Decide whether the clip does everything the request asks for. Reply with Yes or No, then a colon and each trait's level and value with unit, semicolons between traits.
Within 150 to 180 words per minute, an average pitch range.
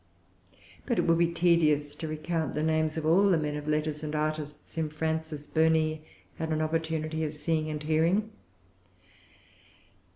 No: average, 160 wpm; narrow, 1.1 semitones